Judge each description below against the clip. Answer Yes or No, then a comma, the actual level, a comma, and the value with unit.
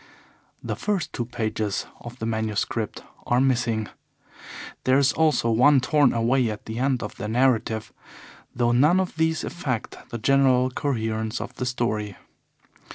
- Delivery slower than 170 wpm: Yes, average, 150 wpm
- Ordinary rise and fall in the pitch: Yes, average, 3.4 semitones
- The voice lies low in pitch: Yes, low, 120 Hz